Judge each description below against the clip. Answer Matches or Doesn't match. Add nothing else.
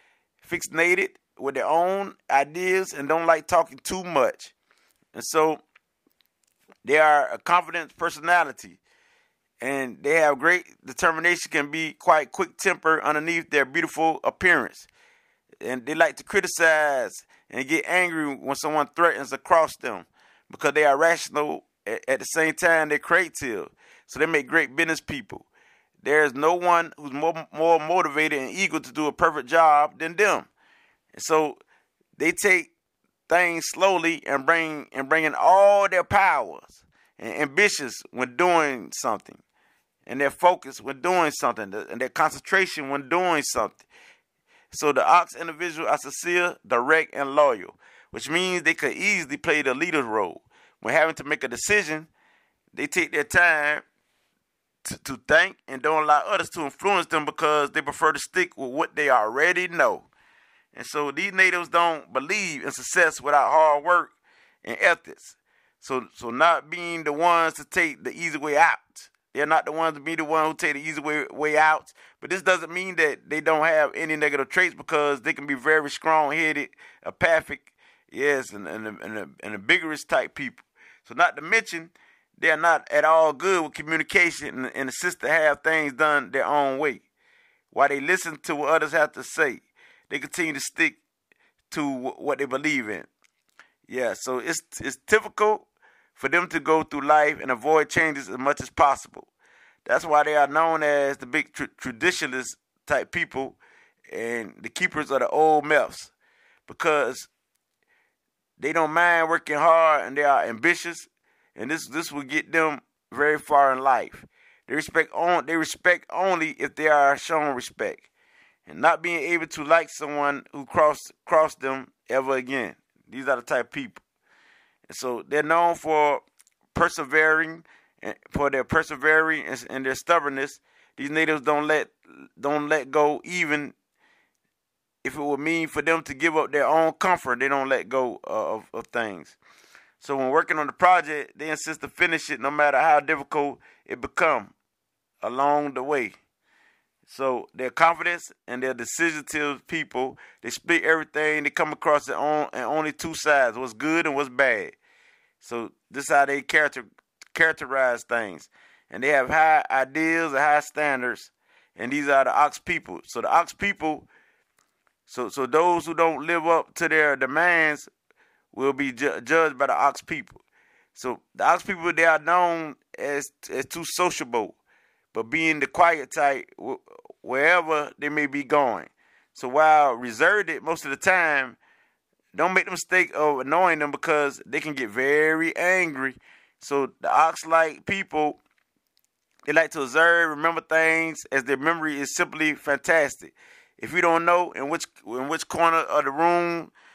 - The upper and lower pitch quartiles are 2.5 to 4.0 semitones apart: Matches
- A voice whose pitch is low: Doesn't match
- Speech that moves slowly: Doesn't match